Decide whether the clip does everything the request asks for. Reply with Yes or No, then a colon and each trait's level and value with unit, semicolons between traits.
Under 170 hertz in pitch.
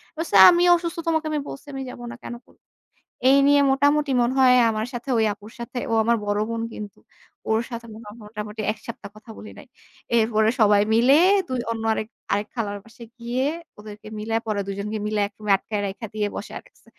No: high, 225 Hz